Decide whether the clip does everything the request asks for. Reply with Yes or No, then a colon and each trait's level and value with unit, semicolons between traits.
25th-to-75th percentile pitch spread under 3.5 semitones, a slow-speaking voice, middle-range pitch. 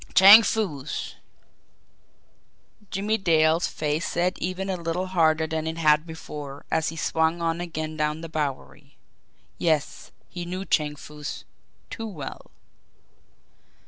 Yes: average, 2.8 semitones; slow, 125 wpm; medium, 160 Hz